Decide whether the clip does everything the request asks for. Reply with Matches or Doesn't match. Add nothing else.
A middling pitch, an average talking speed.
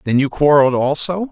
Matches